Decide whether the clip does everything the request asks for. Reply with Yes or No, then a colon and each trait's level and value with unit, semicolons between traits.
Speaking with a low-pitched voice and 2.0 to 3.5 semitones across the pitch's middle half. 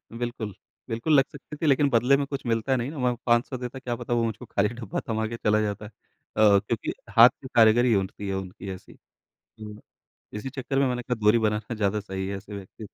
Yes: low, 115 Hz; average, 2.9 semitones